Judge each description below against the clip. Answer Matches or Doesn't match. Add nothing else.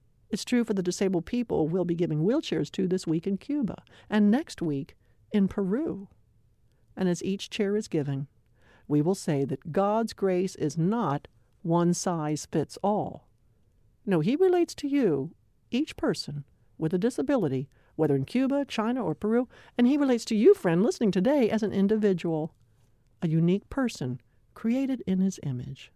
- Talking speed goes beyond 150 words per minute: Matches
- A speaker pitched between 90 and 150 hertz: Doesn't match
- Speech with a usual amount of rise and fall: Doesn't match